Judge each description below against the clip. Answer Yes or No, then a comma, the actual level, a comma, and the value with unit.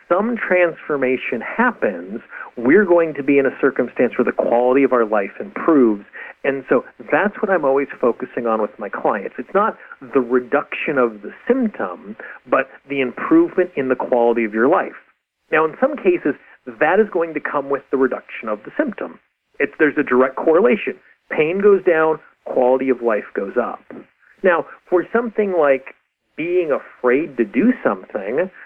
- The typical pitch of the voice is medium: Yes, medium, 145 Hz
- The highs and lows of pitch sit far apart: Yes, wide, 7.1 semitones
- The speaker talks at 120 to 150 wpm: No, average, 170 wpm